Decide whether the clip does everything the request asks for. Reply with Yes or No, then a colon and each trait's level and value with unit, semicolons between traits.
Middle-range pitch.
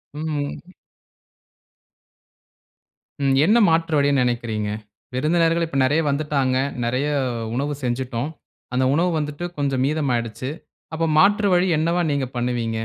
Yes: medium, 145 Hz